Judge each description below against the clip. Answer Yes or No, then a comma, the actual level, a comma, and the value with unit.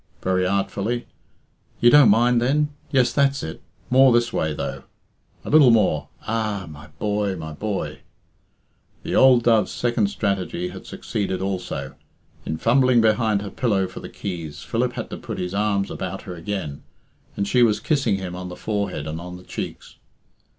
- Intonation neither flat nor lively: Yes, average, 4.5 semitones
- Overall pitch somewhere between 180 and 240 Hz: No, low, 100 Hz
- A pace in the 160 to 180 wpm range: Yes, average, 170 wpm